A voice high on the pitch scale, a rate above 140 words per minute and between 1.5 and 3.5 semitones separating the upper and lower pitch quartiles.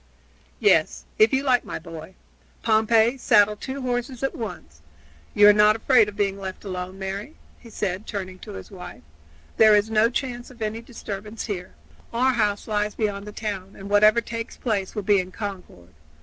Yes: high, 210 Hz; average, 180 wpm; average, 2.9 semitones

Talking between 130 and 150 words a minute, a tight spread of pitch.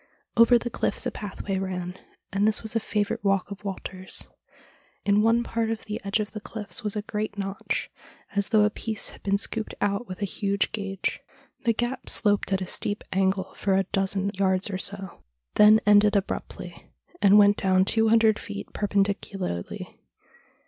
No: average, 180 wpm; narrow, 1.8 semitones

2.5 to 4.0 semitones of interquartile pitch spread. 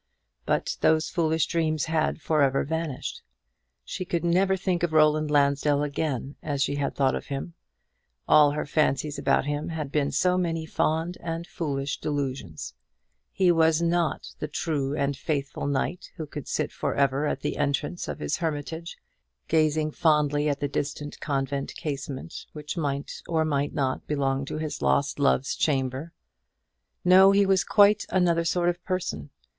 Yes: average, 2.8 semitones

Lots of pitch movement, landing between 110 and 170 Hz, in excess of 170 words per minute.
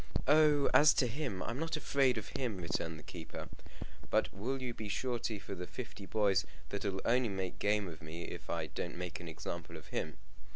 No: wide, 6.4 semitones; low, 100 Hz; average, 200 wpm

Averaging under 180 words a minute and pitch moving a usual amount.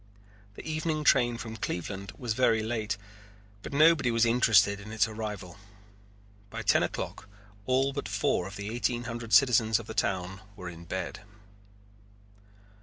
Yes: average, 150 wpm; average, 3.3 semitones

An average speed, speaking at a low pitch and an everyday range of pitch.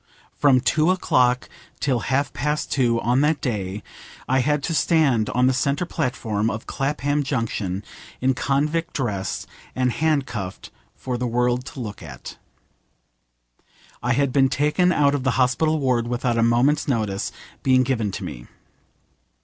Yes: average, 150 wpm; low, 130 Hz; average, 3.4 semitones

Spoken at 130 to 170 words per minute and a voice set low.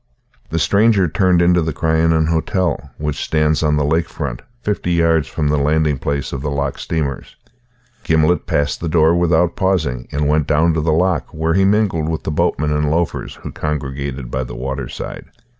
No: average, 185 wpm; very low, 80 Hz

